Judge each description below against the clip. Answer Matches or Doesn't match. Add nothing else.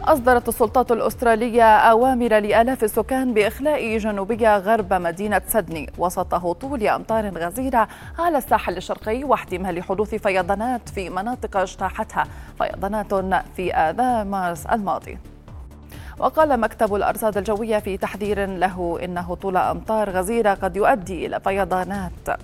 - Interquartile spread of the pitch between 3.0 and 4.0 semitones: Matches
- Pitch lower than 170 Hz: Doesn't match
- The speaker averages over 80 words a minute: Matches